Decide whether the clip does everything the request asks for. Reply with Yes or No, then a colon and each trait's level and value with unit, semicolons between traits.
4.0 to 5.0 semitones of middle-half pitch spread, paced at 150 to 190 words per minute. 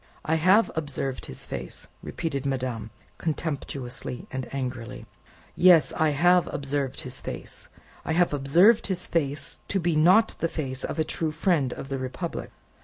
Yes: average, 4.3 semitones; average, 155 wpm